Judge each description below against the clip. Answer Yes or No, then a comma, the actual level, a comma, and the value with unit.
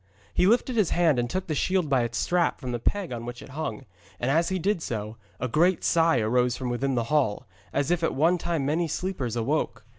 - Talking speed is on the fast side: Yes, fast, 235 wpm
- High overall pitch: No, medium, 145 Hz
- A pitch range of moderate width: No, wide, 6.1 semitones